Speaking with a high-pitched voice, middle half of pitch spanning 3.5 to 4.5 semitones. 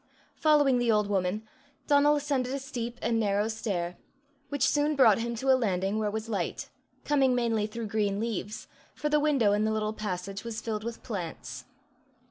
Yes: high, 220 Hz; average, 3.9 semitones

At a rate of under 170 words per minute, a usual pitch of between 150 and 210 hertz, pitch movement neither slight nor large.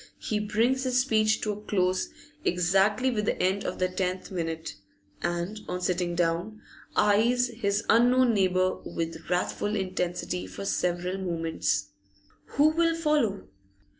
Yes: slow, 135 wpm; high, 190 Hz; average, 3.8 semitones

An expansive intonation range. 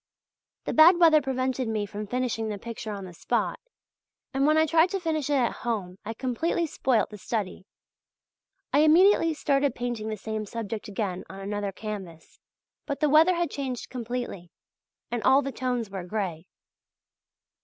Yes: wide, 5.7 semitones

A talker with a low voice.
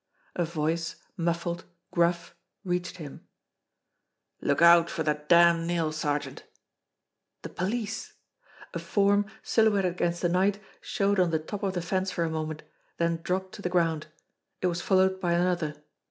No: medium, 175 Hz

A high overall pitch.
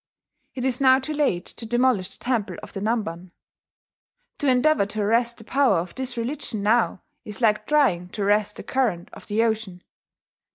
Yes: high, 225 Hz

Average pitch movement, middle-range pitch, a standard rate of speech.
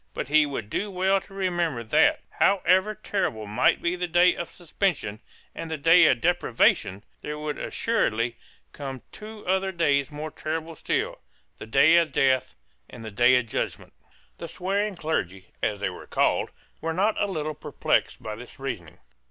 No: wide, 6.7 semitones; medium, 155 Hz; average, 170 wpm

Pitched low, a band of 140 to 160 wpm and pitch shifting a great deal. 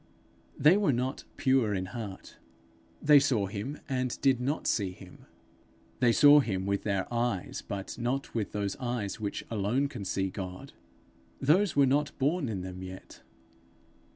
Yes: low, 120 Hz; average, 155 wpm; wide, 5.7 semitones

